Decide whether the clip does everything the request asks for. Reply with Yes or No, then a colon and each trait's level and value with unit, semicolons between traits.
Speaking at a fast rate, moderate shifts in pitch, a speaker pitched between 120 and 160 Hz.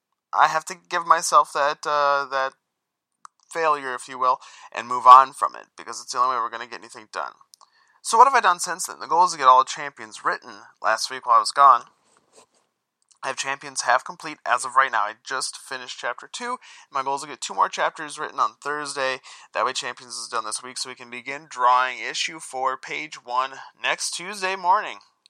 Yes: fast, 225 wpm; average, 3.7 semitones; medium, 140 Hz